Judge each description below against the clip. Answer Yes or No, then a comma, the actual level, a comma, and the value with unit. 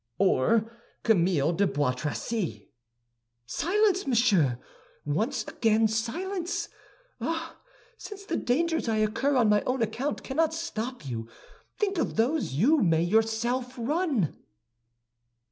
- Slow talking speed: Yes, slow, 115 wpm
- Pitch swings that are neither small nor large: No, wide, 7.5 semitones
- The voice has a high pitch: Yes, high, 230 Hz